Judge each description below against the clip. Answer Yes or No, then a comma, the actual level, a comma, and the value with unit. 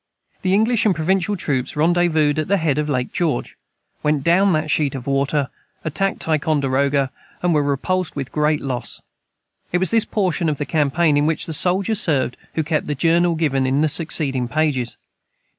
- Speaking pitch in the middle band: Yes, medium, 155 Hz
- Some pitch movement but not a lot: Yes, average, 3.7 semitones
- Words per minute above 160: Yes, average, 180 wpm